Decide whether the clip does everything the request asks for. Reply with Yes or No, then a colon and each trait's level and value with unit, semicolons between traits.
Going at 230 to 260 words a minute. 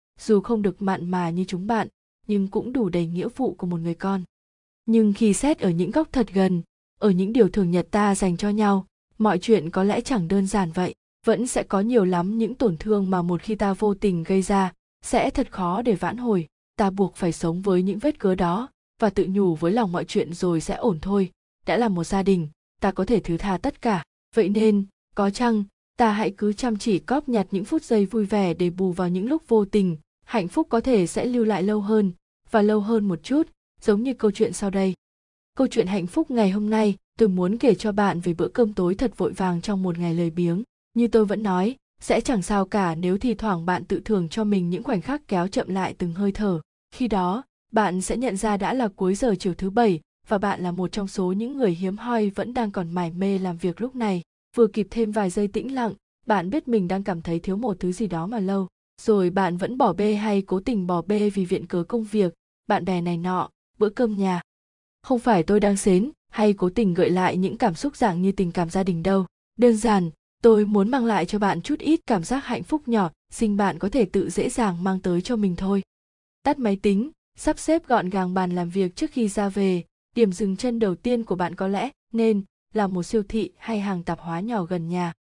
Yes: average, 245 wpm